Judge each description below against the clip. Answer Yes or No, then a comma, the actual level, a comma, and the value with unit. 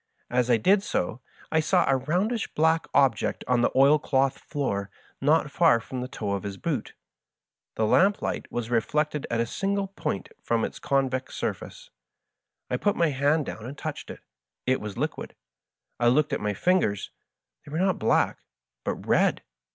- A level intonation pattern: No, wide, 5.6 semitones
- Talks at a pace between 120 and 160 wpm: No, average, 180 wpm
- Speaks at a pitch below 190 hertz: Yes, low, 135 Hz